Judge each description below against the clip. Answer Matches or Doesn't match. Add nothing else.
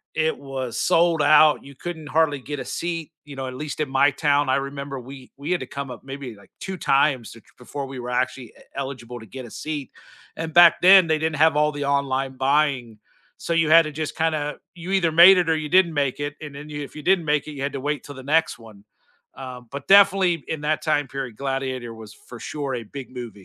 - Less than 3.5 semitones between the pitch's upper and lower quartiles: Matches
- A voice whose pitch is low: Doesn't match